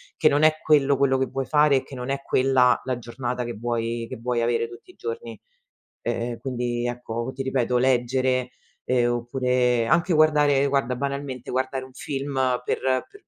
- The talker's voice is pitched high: No, low, 130 Hz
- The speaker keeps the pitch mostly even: Yes, narrow, 2.3 semitones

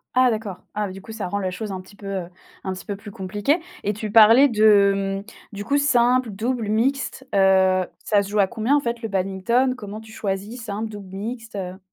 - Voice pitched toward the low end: No, high, 210 Hz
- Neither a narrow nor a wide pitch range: Yes, average, 3.0 semitones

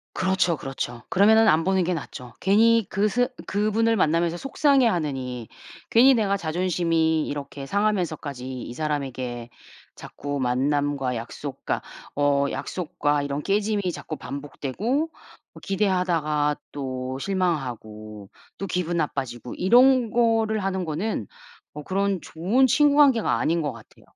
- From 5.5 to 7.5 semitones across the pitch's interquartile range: Yes, wide, 6.4 semitones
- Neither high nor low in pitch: Yes, medium, 165 Hz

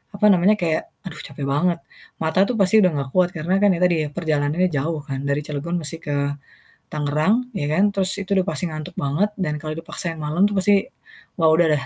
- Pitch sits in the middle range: Yes, medium, 165 Hz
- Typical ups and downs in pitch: Yes, average, 3.5 semitones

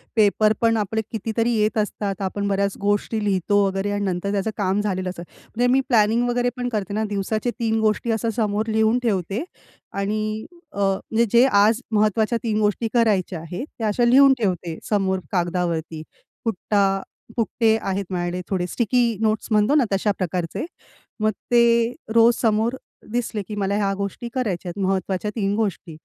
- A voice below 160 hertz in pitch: No, high, 210 Hz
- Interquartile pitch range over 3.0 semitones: No, average, 2.7 semitones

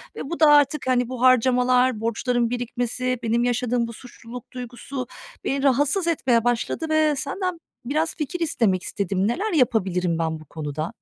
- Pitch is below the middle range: No, very high, 250 Hz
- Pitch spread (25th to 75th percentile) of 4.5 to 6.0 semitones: No, average, 3.6 semitones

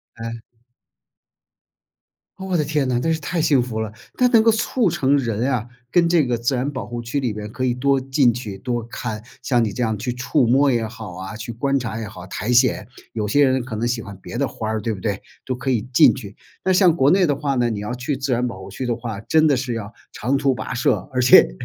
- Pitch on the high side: No, low, 125 Hz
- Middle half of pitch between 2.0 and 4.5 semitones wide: Yes, average, 3.7 semitones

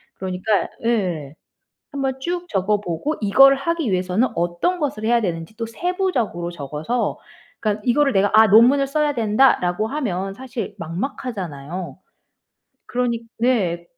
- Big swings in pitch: Yes, wide, 6.6 semitones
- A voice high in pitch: Yes, high, 220 Hz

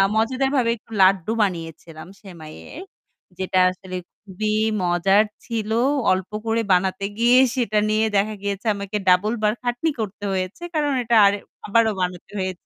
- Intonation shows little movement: No, average, 3.4 semitones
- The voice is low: No, high, 200 Hz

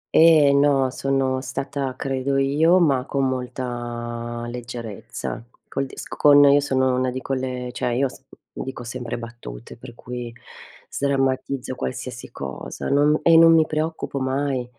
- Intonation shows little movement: Yes, narrow, 2.2 semitones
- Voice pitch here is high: No, low, 130 Hz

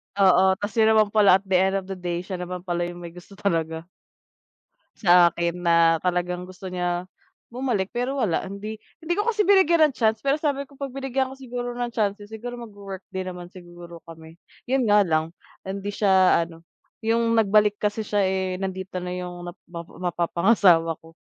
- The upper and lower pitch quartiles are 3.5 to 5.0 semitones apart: Yes, average, 4.1 semitones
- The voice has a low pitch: No, high, 190 Hz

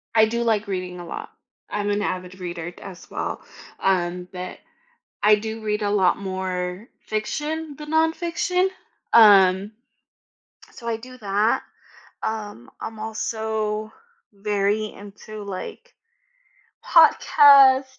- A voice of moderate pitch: No, high, 210 Hz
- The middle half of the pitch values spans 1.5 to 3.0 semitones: No, average, 3.4 semitones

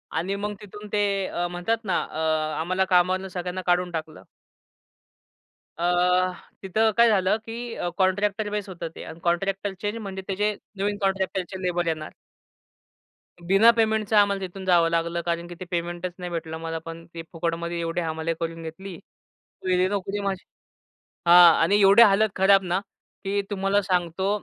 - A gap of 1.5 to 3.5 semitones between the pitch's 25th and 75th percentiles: Yes, average, 2.8 semitones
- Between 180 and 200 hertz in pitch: Yes, medium, 185 Hz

